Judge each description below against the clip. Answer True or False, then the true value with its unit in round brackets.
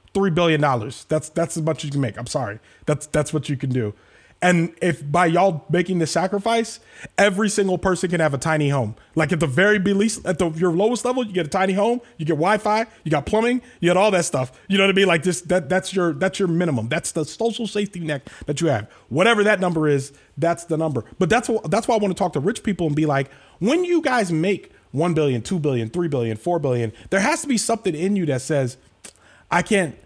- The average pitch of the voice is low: False (175 Hz)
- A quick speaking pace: True (250 wpm)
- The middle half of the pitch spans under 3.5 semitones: False (4.9 semitones)